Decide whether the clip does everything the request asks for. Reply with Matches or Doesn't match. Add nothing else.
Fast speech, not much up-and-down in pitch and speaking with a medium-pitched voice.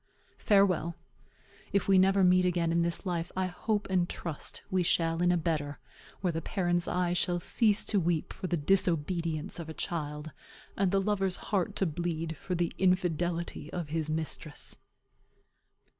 Doesn't match